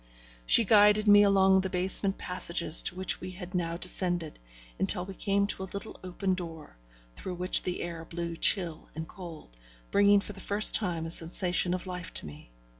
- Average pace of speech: Yes, average, 190 wpm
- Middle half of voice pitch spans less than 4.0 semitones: Yes, narrow, 2.5 semitones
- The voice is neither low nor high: Yes, medium, 180 Hz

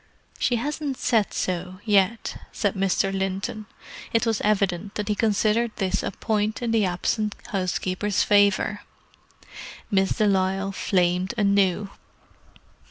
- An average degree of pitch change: No, narrow, 2.2 semitones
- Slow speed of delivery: Yes, slow, 125 wpm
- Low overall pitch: No, high, 200 Hz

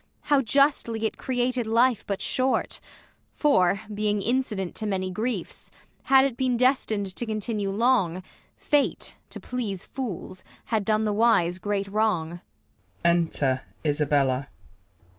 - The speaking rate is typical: No, slow, 120 wpm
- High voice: Yes, high, 220 Hz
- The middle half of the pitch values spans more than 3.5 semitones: Yes, average, 4.2 semitones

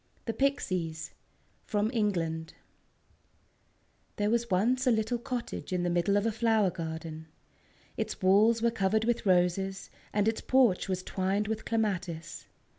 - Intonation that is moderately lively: Yes, average, 3.9 semitones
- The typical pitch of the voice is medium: No, high, 205 Hz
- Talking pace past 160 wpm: No, average, 140 wpm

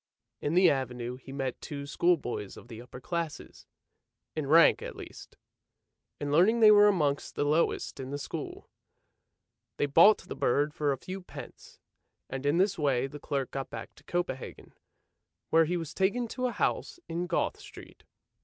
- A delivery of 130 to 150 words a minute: No, average, 175 wpm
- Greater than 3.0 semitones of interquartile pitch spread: Yes, average, 4.7 semitones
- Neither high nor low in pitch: Yes, medium, 145 Hz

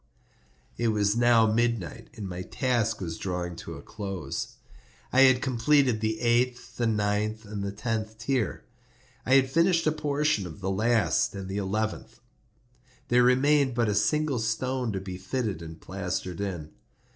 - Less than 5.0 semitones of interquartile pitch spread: Yes, average, 4.1 semitones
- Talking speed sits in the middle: Yes, average, 160 wpm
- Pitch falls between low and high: No, low, 110 Hz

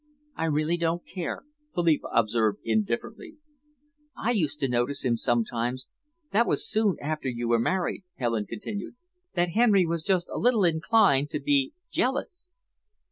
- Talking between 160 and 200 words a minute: No, average, 140 wpm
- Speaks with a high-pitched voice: No, medium, 165 Hz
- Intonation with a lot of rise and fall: Yes, wide, 8.9 semitones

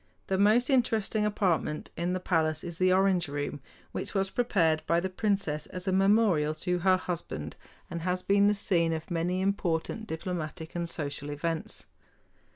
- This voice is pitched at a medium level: Yes, medium, 180 Hz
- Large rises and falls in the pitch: No, average, 3.4 semitones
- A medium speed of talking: Yes, average, 165 wpm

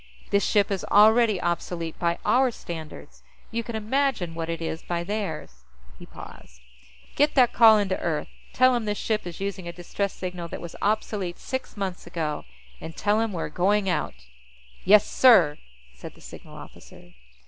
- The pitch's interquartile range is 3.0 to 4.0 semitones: No, average, 4.4 semitones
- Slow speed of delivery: No, average, 175 wpm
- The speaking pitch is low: No, high, 195 Hz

